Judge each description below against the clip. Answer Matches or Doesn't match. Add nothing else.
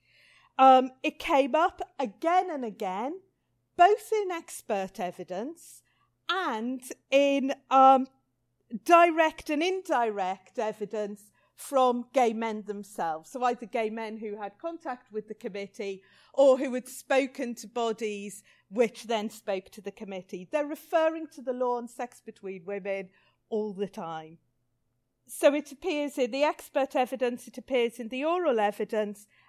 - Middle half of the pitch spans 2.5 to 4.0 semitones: Doesn't match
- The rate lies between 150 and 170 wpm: Doesn't match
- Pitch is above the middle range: Matches